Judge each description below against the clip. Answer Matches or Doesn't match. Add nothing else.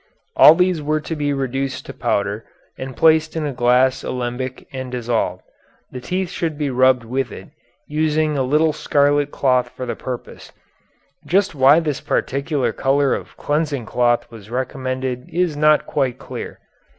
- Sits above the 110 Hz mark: Matches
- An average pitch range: Matches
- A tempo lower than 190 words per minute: Matches